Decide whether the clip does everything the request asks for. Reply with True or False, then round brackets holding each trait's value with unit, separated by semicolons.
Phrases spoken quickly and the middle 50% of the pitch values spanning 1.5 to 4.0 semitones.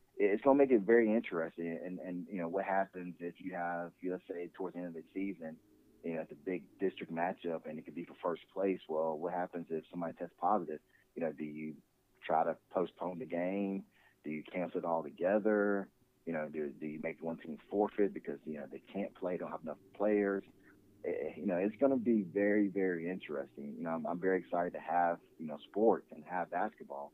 True (225 wpm; 3.4 semitones)